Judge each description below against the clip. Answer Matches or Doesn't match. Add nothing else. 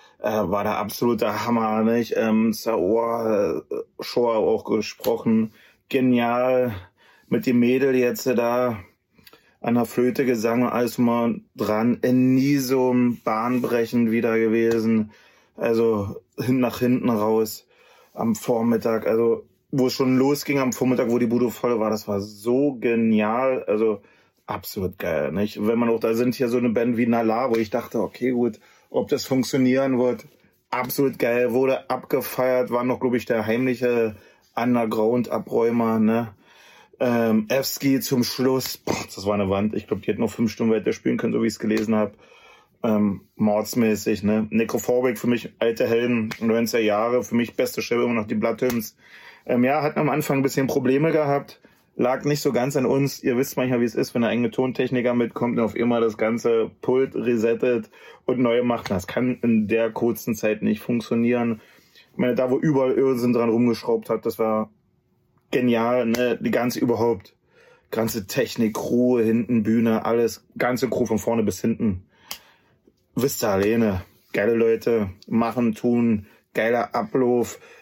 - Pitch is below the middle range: Matches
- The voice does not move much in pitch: Matches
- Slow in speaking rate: Doesn't match